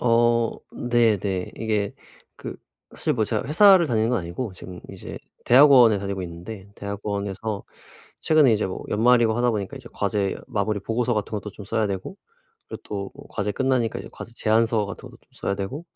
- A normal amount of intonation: Yes, average, 3.1 semitones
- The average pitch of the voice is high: No, low, 110 Hz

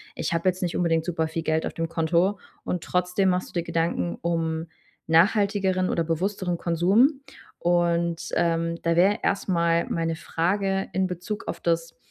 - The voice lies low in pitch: No, medium, 170 Hz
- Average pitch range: No, narrow, 2.0 semitones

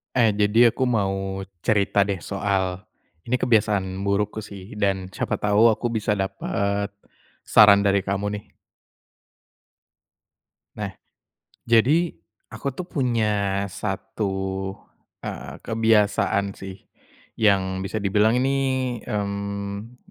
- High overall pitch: No, low, 100 Hz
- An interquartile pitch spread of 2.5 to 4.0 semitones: No, narrow, 2.0 semitones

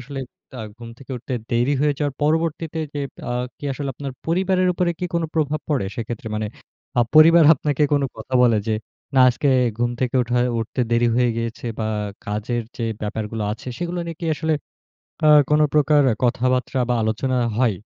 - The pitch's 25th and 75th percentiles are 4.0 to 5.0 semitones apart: Yes, average, 4.4 semitones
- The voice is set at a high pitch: No, low, 130 Hz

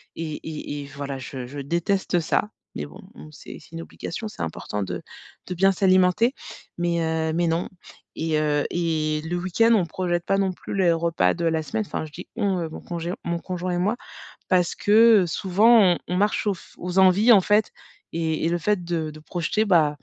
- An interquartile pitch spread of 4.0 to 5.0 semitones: No, average, 3.3 semitones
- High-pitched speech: No, medium, 170 Hz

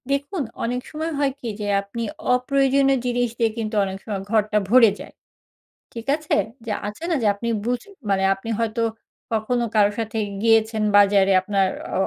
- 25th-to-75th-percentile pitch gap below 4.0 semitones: Yes, average, 3.3 semitones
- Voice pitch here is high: Yes, high, 230 Hz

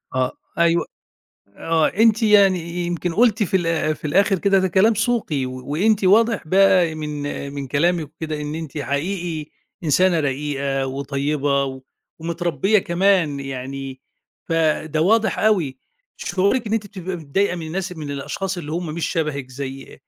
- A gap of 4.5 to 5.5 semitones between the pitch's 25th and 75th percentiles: Yes, average, 5.0 semitones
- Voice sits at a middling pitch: Yes, medium, 165 Hz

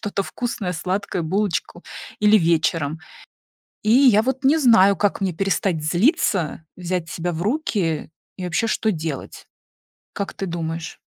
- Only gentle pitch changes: No, average, 4.4 semitones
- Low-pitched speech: No, medium, 185 Hz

